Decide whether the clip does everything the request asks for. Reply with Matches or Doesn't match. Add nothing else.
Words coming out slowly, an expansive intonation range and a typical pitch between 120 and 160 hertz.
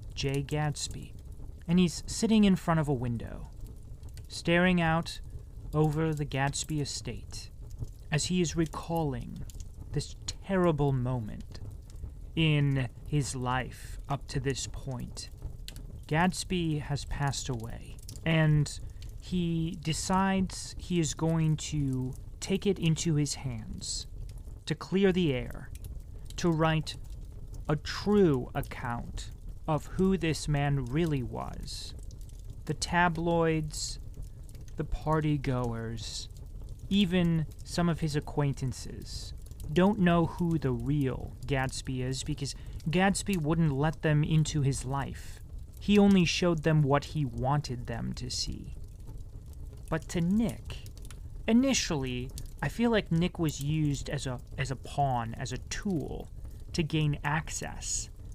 Matches